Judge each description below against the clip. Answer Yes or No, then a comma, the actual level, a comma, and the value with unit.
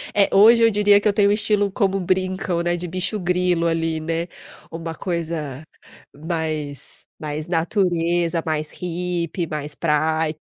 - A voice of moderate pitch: Yes, medium, 170 Hz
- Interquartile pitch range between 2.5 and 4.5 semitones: Yes, average, 2.8 semitones